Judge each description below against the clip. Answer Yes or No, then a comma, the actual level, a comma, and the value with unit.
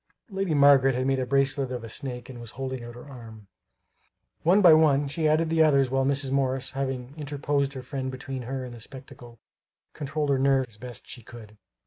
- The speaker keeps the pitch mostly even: Yes, narrow, 2.1 semitones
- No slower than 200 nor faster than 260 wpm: Yes, fast, 205 wpm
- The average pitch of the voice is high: No, low, 135 Hz